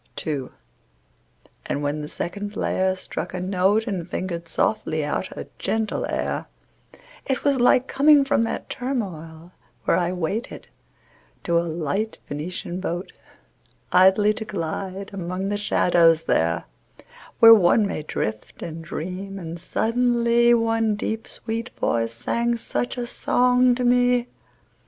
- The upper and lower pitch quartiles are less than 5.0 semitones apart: No, wide, 5.4 semitones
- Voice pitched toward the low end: No, high, 195 Hz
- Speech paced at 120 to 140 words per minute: Yes, slow, 135 wpm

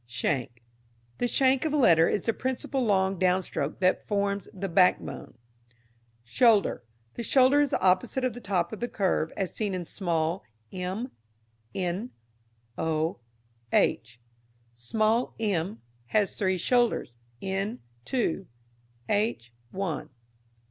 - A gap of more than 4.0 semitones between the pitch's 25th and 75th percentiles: Yes, average, 5.0 semitones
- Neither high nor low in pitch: No, high, 195 Hz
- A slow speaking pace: Yes, slow, 130 wpm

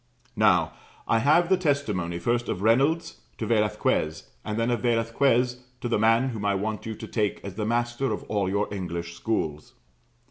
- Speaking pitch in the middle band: No, low, 115 Hz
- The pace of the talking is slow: No, average, 180 wpm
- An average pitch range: Yes, average, 3.2 semitones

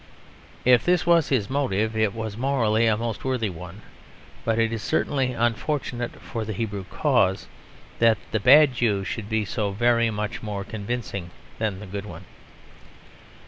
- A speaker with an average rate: Yes, average, 160 wpm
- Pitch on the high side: No, low, 110 Hz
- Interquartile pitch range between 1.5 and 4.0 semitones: Yes, average, 2.8 semitones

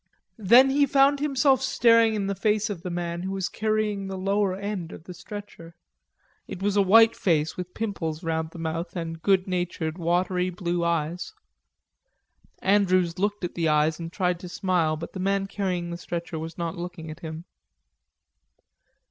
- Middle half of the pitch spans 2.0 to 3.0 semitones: No, average, 3.4 semitones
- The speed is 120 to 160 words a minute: No, average, 175 wpm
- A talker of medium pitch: Yes, medium, 180 Hz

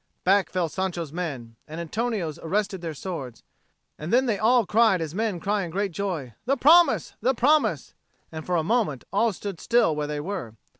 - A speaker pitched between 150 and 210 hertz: Yes, medium, 185 Hz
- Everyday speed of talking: Yes, average, 190 wpm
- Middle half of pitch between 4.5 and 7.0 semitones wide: Yes, wide, 5.6 semitones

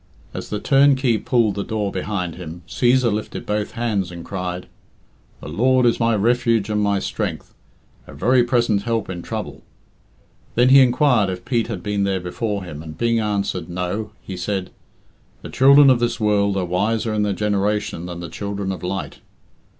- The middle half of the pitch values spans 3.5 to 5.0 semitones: Yes, average, 4.0 semitones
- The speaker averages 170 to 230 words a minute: Yes, average, 180 wpm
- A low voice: Yes, low, 105 Hz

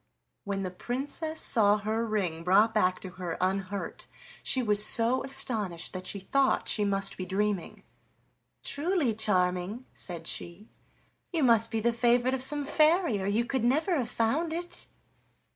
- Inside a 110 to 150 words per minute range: No, average, 160 wpm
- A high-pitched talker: Yes, high, 220 Hz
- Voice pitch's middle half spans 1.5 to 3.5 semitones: No, average, 5.3 semitones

